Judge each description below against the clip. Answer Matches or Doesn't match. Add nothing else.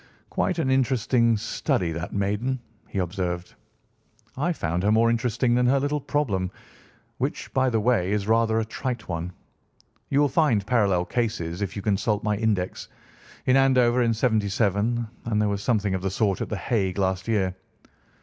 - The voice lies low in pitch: Matches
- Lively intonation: Doesn't match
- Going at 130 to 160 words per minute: Doesn't match